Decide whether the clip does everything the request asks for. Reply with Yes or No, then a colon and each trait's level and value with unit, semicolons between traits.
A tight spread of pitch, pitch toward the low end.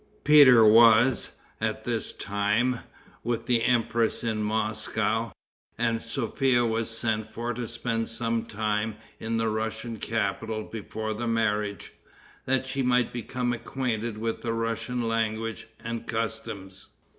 Yes: narrow, 1.4 semitones; low, 115 Hz